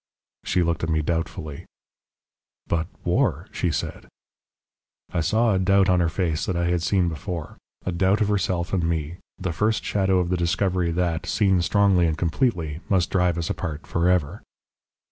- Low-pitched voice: Yes, very low, 90 Hz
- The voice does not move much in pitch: Yes, narrow, 2.3 semitones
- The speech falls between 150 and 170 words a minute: No, average, 180 wpm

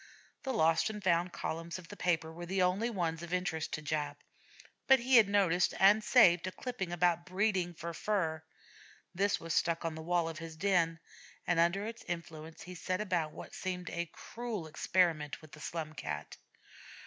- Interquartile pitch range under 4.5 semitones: Yes, average, 2.9 semitones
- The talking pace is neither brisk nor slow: Yes, average, 185 wpm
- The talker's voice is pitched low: No, medium, 175 Hz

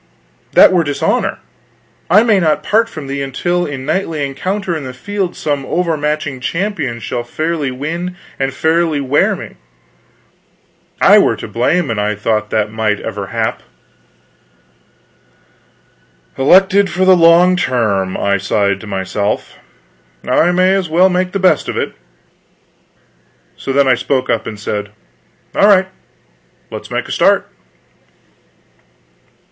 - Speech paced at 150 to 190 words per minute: No, average, 140 wpm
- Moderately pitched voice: Yes, medium, 145 Hz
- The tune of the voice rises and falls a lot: Yes, wide, 7.4 semitones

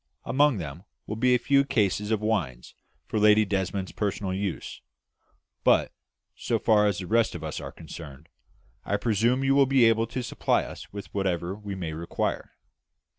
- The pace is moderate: Yes, average, 175 wpm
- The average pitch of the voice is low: Yes, low, 105 Hz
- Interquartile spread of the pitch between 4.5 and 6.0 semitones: No, average, 3.8 semitones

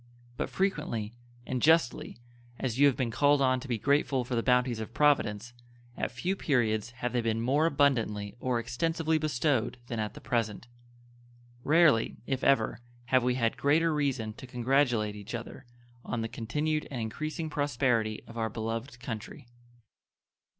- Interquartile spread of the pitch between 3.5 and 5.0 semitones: Yes, average, 4.0 semitones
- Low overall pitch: Yes, low, 125 Hz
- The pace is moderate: Yes, average, 160 wpm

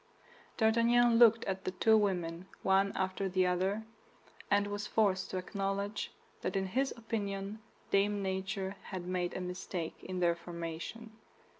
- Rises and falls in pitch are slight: Yes, narrow, 2.2 semitones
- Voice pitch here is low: No, high, 195 Hz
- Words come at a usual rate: Yes, average, 145 wpm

